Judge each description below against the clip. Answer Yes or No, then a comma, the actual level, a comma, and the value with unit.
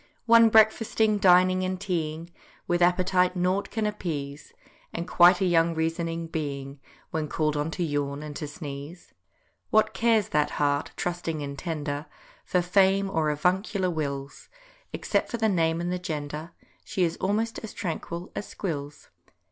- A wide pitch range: No, average, 3.8 semitones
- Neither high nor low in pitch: Yes, medium, 170 Hz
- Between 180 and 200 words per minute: No, average, 155 wpm